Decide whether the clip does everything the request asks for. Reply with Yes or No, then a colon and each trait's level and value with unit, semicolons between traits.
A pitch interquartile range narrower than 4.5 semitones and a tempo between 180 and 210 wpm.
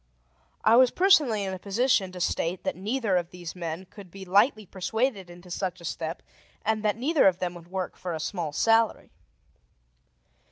Yes: average, 3.9 semitones; average, 185 wpm